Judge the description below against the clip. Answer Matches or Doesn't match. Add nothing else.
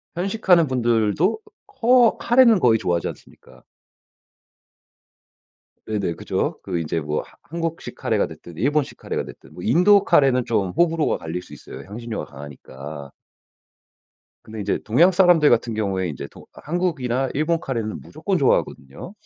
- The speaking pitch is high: Doesn't match